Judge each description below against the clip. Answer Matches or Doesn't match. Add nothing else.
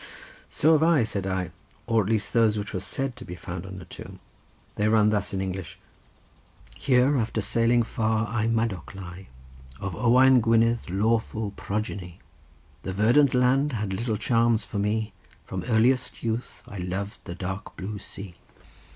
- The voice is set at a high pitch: Doesn't match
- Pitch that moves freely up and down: Doesn't match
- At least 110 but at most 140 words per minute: Doesn't match